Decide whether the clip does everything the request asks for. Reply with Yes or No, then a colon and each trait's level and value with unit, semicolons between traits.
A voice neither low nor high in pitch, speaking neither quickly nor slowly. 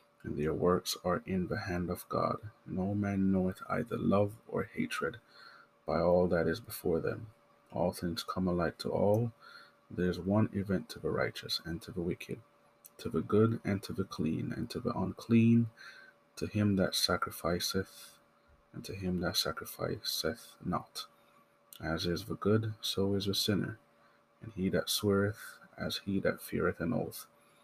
No: very low, 95 Hz; average, 170 wpm